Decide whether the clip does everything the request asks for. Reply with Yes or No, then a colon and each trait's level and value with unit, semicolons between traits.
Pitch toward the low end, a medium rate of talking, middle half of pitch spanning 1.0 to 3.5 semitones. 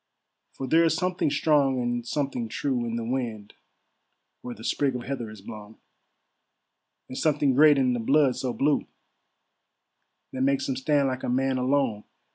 Yes: low, 130 Hz; average, 160 wpm; average, 2.8 semitones